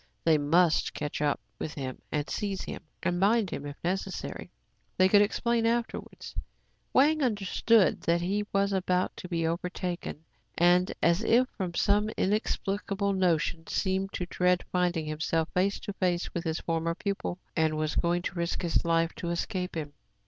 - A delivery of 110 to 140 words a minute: No, average, 165 wpm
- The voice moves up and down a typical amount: Yes, average, 3.0 semitones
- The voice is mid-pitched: Yes, medium, 180 Hz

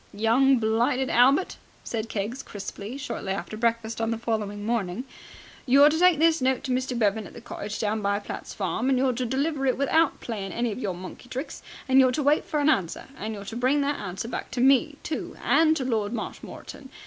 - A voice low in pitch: No, high, 245 Hz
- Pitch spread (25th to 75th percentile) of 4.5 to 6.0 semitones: No, average, 4.0 semitones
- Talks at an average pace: No, fast, 215 wpm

